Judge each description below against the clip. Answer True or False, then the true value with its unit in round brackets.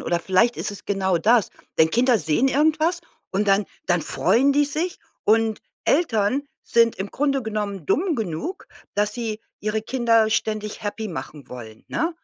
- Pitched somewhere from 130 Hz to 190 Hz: False (220 Hz)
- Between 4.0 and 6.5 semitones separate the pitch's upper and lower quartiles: True (5.1 semitones)